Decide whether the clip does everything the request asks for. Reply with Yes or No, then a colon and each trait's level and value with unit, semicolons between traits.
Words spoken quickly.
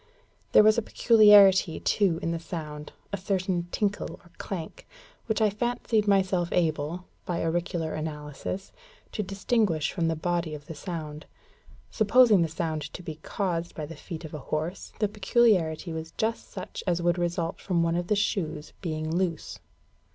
No: average, 165 wpm